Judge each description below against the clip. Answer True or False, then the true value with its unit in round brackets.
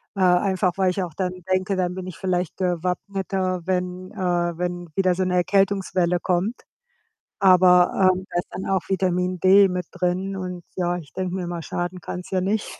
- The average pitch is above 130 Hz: True (185 Hz)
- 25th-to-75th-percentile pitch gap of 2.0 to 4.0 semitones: False (1.0 semitones)